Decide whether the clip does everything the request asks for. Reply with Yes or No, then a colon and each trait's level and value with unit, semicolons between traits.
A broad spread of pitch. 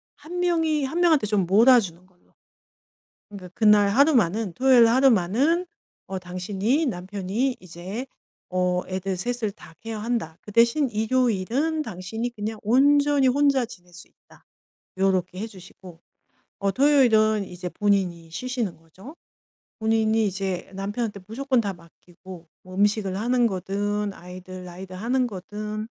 No: average, 5.0 semitones